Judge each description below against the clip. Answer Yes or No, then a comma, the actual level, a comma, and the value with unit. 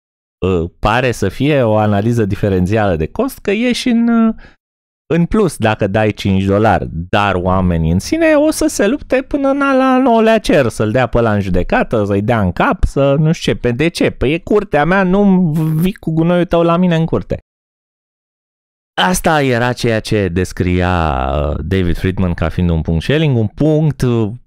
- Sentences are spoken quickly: Yes, fast, 180 wpm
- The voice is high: No, low, 115 Hz